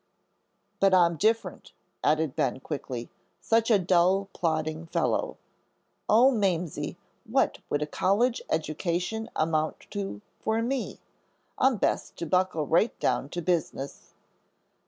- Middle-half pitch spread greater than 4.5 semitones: Yes, average, 4.9 semitones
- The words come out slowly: Yes, slow, 120 wpm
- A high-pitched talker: No, medium, 175 Hz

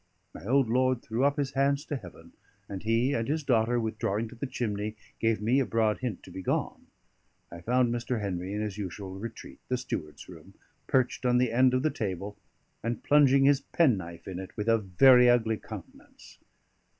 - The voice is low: Yes, low, 115 Hz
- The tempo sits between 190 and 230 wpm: Yes, average, 195 wpm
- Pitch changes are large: No, average, 3.8 semitones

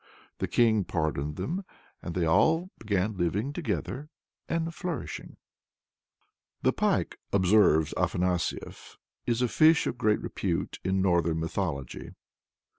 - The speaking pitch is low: Yes, low, 100 Hz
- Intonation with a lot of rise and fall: Yes, wide, 6.7 semitones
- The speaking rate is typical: No, slow, 115 wpm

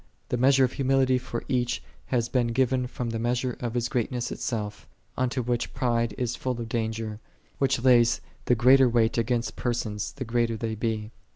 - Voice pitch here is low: Yes, low, 120 Hz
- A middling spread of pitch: No, narrow, 1.7 semitones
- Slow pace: No, average, 185 wpm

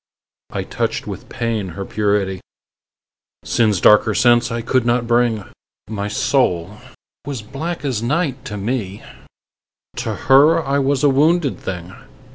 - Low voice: Yes, low, 120 Hz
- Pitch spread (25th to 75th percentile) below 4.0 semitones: No, average, 4.8 semitones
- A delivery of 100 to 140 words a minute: Yes, slow, 135 wpm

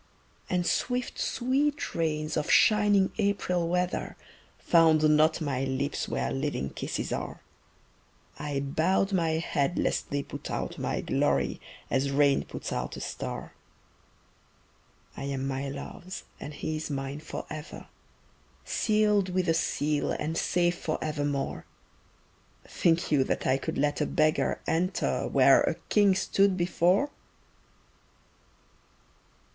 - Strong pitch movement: No, average, 4.4 semitones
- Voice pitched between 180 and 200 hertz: No, medium, 155 Hz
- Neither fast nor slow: No, slow, 125 wpm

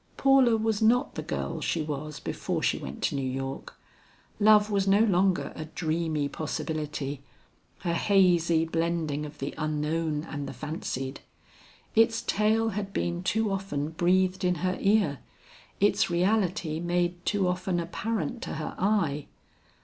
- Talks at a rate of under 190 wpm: Yes, average, 145 wpm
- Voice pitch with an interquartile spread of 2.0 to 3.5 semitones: No, average, 4.8 semitones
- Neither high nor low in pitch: Yes, medium, 175 Hz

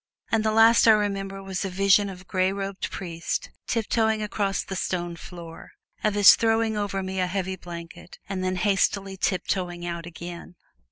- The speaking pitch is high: Yes, high, 195 Hz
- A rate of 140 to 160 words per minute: No, average, 175 wpm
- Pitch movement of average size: No, narrow, 2.3 semitones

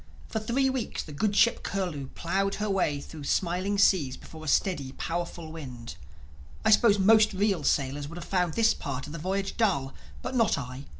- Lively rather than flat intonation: Yes, wide, 5.9 semitones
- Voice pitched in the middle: Yes, medium, 180 Hz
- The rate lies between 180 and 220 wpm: Yes, average, 190 wpm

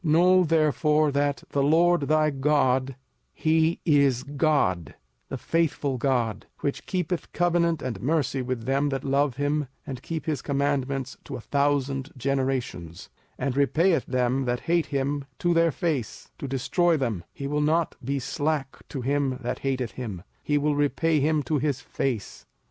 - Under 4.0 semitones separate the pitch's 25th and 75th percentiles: Yes, average, 2.8 semitones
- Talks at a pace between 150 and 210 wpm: Yes, average, 165 wpm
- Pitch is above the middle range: No, medium, 140 Hz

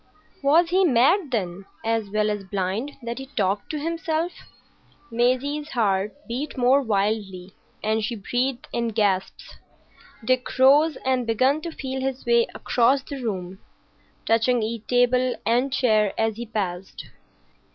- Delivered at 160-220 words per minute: No, average, 140 wpm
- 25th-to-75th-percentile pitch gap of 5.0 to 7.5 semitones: No, average, 4.1 semitones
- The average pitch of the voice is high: Yes, high, 240 Hz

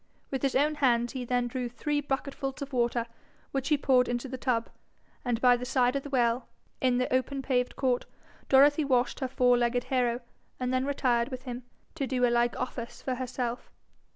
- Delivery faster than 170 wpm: Yes, average, 200 wpm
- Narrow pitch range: Yes, narrow, 1.7 semitones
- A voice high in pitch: Yes, very high, 255 Hz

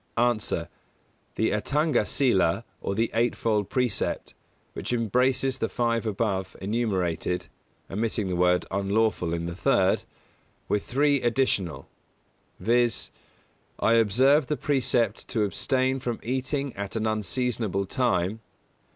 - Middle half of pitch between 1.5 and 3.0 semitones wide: No, average, 4.3 semitones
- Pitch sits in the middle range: No, low, 115 Hz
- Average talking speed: No, slow, 120 wpm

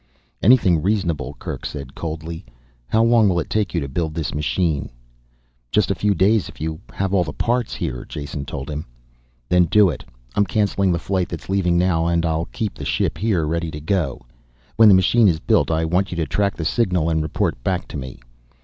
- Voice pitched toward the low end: Yes, very low, 85 Hz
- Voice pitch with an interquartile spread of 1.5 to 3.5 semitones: No, average, 4.0 semitones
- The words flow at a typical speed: No, fast, 210 wpm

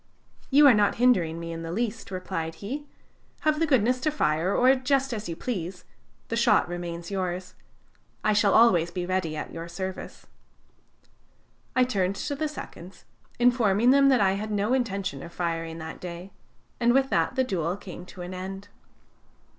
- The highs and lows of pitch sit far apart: Yes, wide, 6.0 semitones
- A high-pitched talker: Yes, high, 195 Hz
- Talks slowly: No, average, 175 wpm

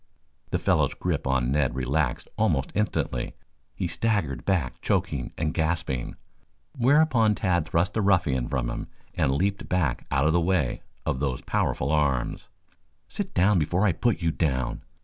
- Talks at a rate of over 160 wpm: No, average, 155 wpm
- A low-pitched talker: Yes, very low, 80 Hz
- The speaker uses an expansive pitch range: Yes, wide, 6.1 semitones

